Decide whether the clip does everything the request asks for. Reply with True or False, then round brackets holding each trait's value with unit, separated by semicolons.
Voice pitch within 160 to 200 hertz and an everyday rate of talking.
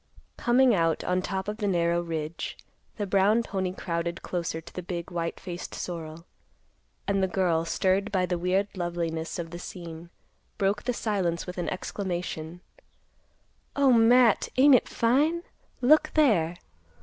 True (185 Hz; 150 wpm)